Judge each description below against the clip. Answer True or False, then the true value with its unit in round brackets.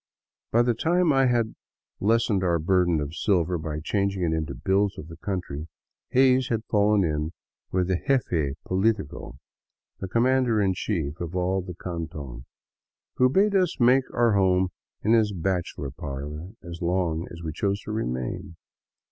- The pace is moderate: True (160 wpm)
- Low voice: True (95 Hz)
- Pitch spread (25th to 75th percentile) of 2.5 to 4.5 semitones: False (5.3 semitones)